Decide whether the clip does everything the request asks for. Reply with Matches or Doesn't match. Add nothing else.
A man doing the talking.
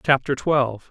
Matches